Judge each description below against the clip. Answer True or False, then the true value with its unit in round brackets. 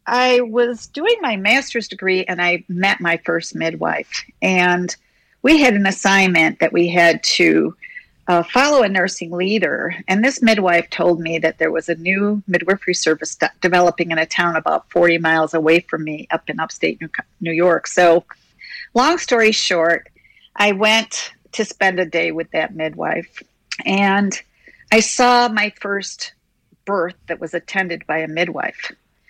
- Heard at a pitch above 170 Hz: True (185 Hz)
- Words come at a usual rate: True (165 wpm)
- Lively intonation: False (4.2 semitones)